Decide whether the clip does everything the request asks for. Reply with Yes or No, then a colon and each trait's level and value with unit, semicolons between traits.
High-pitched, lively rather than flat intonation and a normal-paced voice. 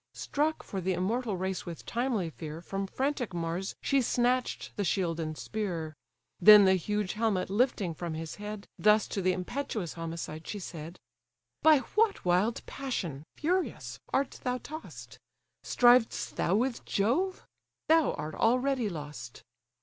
Yes: high, 205 Hz; wide, 6.5 semitones; average, 145 wpm